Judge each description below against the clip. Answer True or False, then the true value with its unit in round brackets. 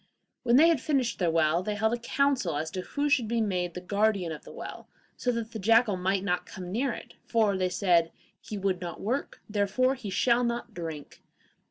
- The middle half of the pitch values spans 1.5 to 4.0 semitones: False (4.8 semitones)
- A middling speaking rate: False (215 wpm)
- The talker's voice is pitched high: True (205 Hz)